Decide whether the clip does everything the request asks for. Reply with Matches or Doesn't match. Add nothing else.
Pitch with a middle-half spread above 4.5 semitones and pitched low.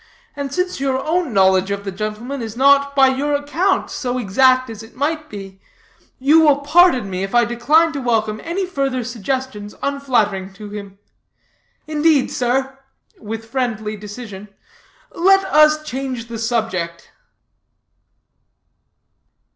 Doesn't match